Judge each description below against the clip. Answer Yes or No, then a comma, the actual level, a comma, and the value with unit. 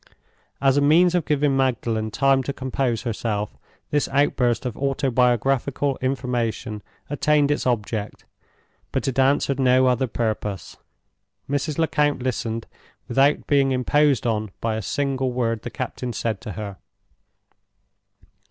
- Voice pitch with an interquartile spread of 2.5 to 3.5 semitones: Yes, average, 3.2 semitones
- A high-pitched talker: No, low, 130 Hz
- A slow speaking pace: Yes, slow, 130 wpm